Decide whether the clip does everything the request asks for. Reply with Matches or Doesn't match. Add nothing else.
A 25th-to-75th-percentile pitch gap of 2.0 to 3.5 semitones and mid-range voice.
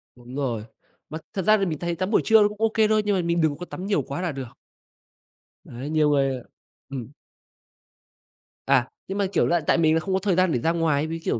Doesn't match